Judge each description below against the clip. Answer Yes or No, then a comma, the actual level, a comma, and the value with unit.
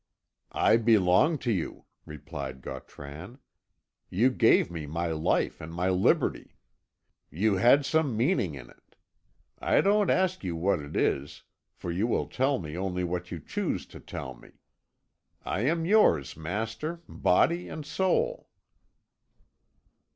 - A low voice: Yes, very low, 95 Hz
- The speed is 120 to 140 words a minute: Yes, slow, 135 wpm